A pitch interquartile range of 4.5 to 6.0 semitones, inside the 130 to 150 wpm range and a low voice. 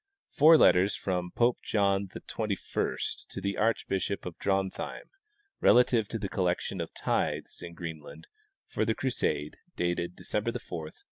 No: average, 3.8 semitones; average, 140 wpm; very low, 95 Hz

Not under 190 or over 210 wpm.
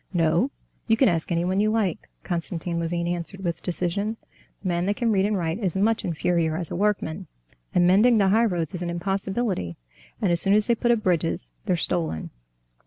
Yes: average, 195 wpm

